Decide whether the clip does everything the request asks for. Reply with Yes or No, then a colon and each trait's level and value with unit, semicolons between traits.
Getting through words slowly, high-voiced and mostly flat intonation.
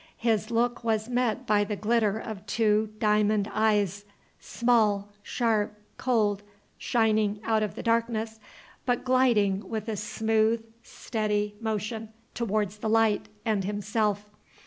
Yes: slow, 125 wpm; high, 215 Hz; narrow, 1.5 semitones